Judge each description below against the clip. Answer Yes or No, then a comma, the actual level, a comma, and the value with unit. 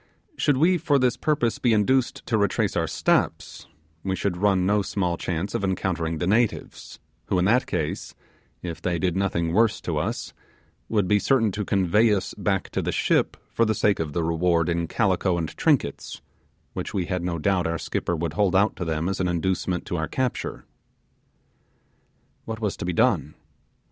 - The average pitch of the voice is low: Yes, very low, 95 Hz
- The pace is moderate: Yes, average, 190 wpm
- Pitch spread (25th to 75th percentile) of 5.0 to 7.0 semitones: No, average, 3.7 semitones